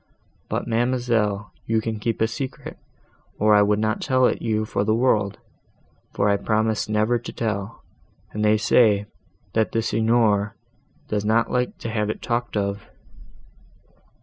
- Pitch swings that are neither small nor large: No, narrow, 1.8 semitones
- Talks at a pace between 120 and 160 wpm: Yes, average, 155 wpm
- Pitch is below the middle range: Yes, low, 110 Hz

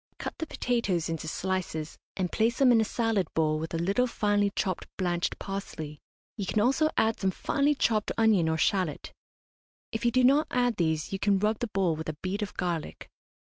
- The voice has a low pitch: No, high, 195 Hz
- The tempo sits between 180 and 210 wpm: Yes, average, 200 wpm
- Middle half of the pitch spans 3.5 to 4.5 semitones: No, average, 5.0 semitones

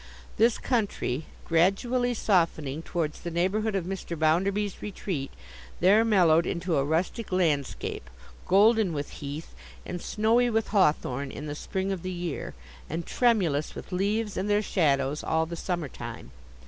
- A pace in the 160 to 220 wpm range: No, average, 145 wpm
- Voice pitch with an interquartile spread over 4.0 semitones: Yes, average, 4.8 semitones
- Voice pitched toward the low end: No, medium, 180 Hz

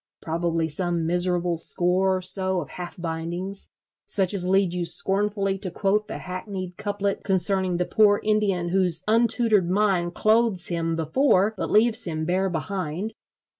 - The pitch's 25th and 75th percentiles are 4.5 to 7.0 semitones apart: No, narrow, 2.6 semitones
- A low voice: No, medium, 185 Hz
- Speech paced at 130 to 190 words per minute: Yes, average, 150 wpm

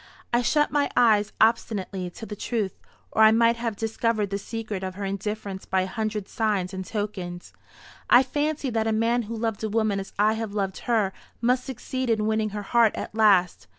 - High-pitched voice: Yes, high, 220 Hz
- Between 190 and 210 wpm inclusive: Yes, average, 195 wpm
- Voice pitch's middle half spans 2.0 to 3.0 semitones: Yes, narrow, 2.5 semitones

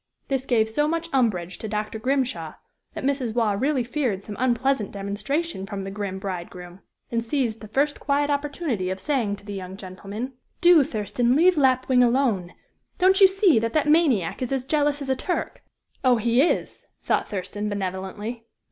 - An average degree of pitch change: No, wide, 5.7 semitones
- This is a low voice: No, high, 235 Hz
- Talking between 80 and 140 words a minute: No, average, 175 wpm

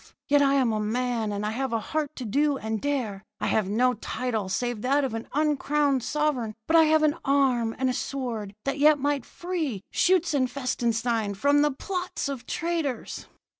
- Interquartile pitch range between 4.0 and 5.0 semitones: Yes, average, 4.5 semitones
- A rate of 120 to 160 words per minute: No, average, 185 wpm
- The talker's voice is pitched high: Yes, very high, 260 Hz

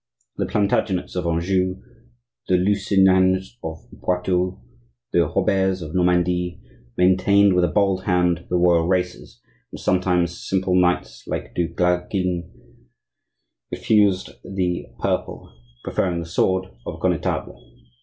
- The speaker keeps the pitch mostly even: Yes, narrow, 1.2 semitones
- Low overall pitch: Yes, very low, 90 Hz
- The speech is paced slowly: Yes, slow, 120 wpm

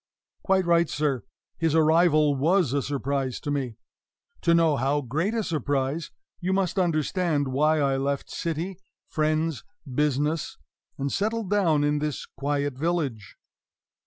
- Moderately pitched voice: Yes, medium, 150 Hz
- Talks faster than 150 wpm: No, slow, 135 wpm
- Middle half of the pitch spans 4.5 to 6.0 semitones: No, average, 3.2 semitones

